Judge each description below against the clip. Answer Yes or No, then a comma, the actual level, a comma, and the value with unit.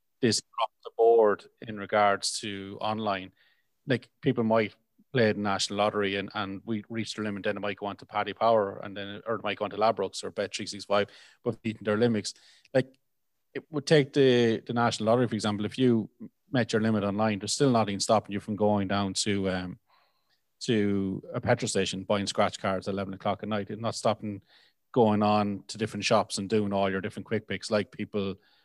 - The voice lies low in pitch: Yes, low, 105 Hz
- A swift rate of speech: Yes, fast, 210 wpm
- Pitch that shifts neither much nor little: No, narrow, 2.1 semitones